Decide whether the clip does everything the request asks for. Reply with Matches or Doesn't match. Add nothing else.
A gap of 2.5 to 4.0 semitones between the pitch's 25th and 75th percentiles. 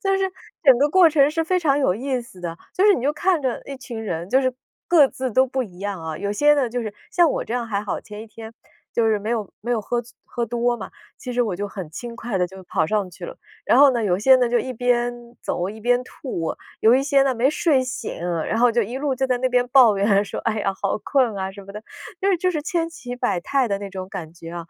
Doesn't match